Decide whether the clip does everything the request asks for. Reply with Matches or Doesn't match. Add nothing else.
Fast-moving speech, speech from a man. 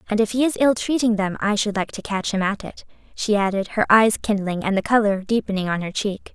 Doesn't match